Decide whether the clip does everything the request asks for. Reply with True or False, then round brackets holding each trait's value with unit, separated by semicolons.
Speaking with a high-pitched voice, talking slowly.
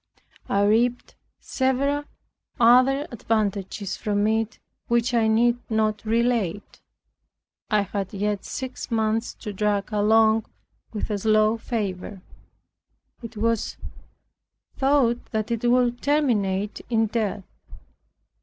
True (220 Hz; 105 wpm)